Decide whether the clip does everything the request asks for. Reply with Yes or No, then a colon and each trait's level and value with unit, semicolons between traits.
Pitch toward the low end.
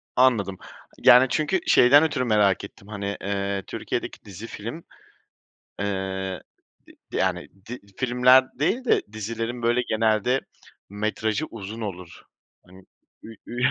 Yes: low, 110 Hz